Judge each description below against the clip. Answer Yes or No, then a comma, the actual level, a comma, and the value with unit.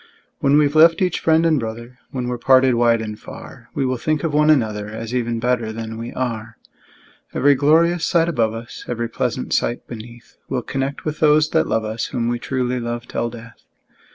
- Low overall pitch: Yes, low, 125 Hz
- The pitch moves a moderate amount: Yes, average, 4.3 semitones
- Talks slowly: No, average, 200 wpm